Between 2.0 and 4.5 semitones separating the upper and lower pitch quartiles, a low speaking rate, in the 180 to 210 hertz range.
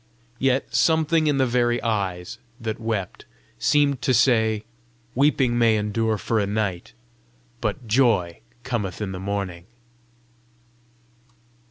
No: average, 3.9 semitones; slow, 120 wpm; low, 115 Hz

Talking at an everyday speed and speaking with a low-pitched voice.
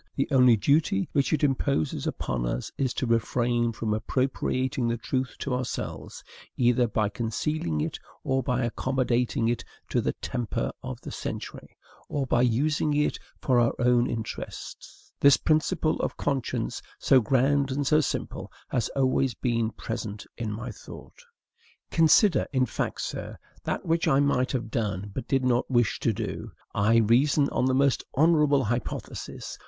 Yes: average, 160 wpm; low, 125 Hz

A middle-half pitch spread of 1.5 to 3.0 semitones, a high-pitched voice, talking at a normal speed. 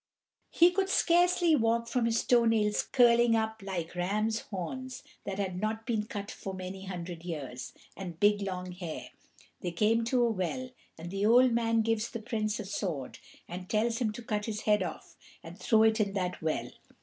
No: average, 3.7 semitones; high, 215 Hz; average, 190 wpm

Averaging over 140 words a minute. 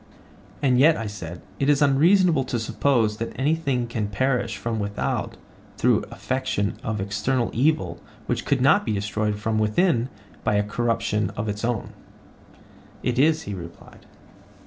Yes: average, 150 wpm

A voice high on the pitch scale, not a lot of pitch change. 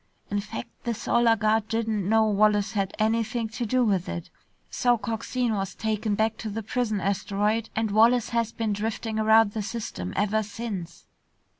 Yes: high, 220 Hz; narrow, 1.9 semitones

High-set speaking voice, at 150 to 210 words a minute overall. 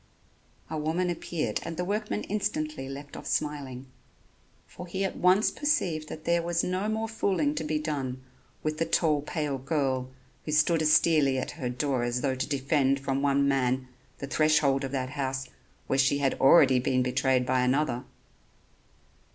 No: medium, 145 Hz; average, 170 wpm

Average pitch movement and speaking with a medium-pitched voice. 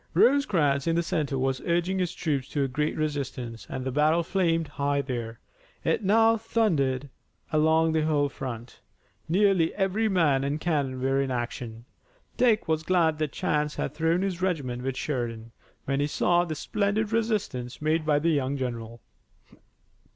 Yes: average, 4.7 semitones; medium, 150 Hz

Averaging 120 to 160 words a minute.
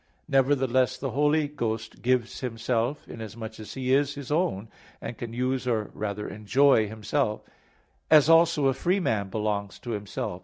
Yes: average, 155 wpm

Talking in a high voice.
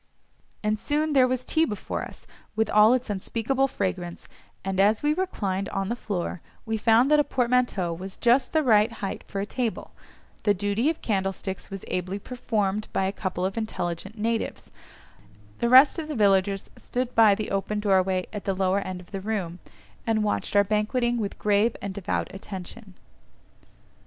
Yes: high, 210 Hz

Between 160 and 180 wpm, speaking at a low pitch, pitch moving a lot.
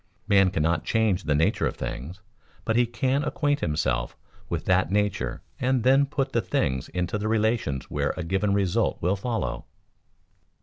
Yes: average, 165 wpm; low, 100 Hz; wide, 5.8 semitones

